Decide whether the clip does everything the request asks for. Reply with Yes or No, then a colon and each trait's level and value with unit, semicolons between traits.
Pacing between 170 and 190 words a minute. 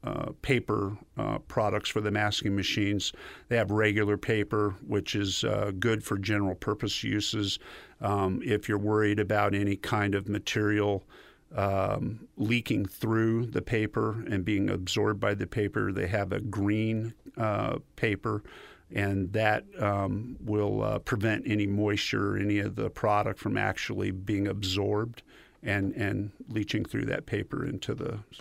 No: average, 150 wpm